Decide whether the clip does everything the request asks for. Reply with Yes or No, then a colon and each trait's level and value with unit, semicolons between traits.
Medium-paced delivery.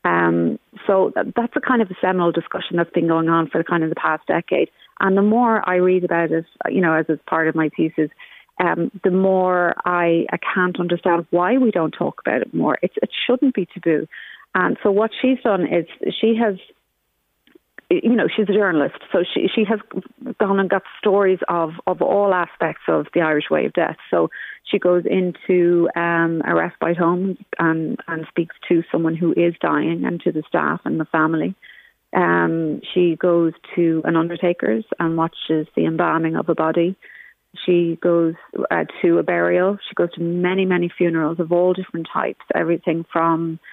Yes: average, 190 wpm